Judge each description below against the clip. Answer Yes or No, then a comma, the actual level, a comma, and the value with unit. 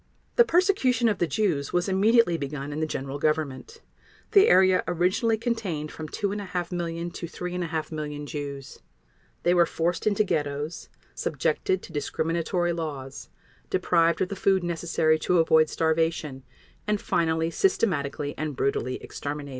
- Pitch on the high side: No, medium, 165 Hz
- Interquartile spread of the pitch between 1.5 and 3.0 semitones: No, average, 3.9 semitones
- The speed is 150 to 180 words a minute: No, average, 140 wpm